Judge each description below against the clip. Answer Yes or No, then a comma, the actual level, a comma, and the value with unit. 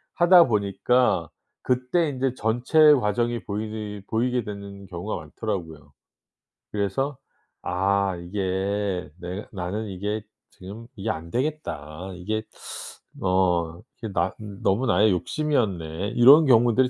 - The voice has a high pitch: No, low, 105 Hz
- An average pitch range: Yes, average, 4.7 semitones